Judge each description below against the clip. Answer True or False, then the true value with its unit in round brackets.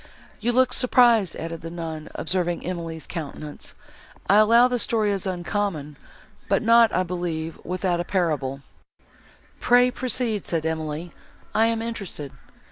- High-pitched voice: False (180 Hz)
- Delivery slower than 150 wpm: True (135 wpm)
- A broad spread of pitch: True (5.7 semitones)